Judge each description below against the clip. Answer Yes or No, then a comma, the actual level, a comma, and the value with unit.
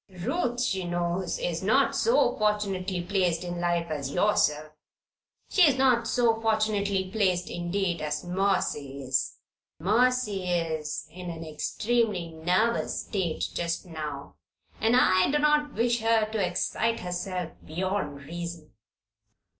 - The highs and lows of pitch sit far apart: No, average, 4.6 semitones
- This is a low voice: No, medium, 185 Hz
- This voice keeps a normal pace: No, slow, 130 wpm